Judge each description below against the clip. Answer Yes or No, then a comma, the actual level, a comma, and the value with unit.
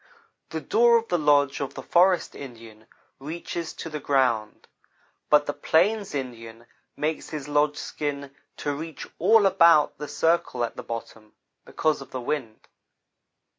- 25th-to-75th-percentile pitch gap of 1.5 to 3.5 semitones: No, average, 4.1 semitones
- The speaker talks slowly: No, average, 150 wpm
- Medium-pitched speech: Yes, medium, 145 Hz